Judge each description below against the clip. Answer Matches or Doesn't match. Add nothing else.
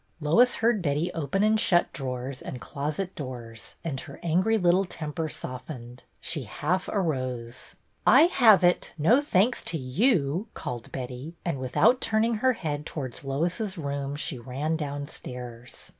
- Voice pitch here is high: Doesn't match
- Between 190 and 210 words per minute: Doesn't match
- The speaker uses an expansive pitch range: Matches